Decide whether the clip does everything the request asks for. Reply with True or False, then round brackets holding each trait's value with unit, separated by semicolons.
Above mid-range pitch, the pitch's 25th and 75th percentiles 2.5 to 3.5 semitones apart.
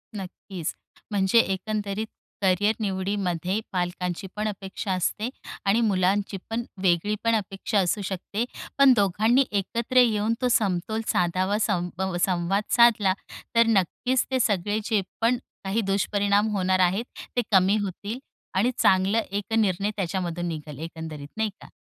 True (200 Hz; 2.8 semitones)